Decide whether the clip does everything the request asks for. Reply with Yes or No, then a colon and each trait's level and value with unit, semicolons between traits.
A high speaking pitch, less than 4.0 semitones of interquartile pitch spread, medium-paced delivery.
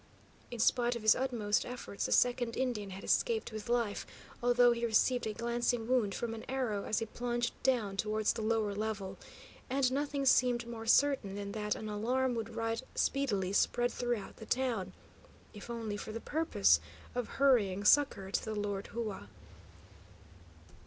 Yes: high, 230 Hz; average, 2.8 semitones; average, 165 wpm